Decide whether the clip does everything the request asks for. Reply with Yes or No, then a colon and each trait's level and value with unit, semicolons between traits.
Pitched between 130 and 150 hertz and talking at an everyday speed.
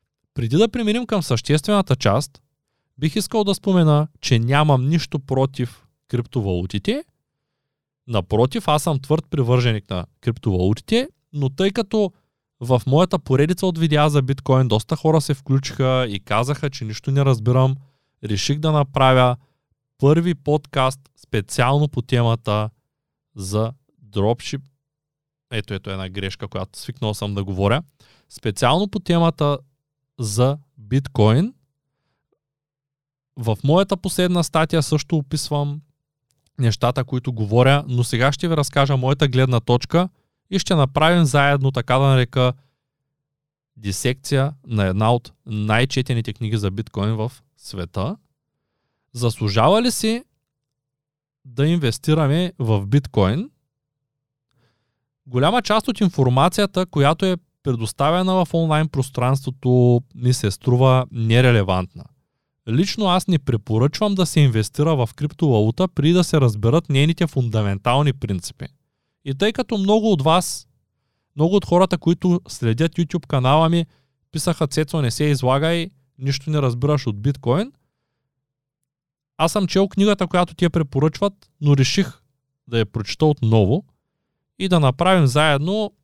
Yes: medium, 140 Hz; average, 125 wpm